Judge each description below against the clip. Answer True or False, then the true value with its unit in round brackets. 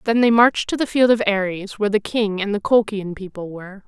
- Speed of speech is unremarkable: False (250 wpm)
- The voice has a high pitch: True (210 Hz)